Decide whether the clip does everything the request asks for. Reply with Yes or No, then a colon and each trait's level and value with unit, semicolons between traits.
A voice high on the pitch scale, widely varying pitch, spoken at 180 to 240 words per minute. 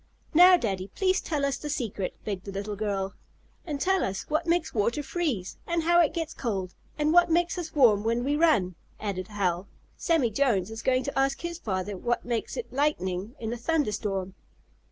Yes: high, 240 Hz; wide, 7.9 semitones; average, 195 wpm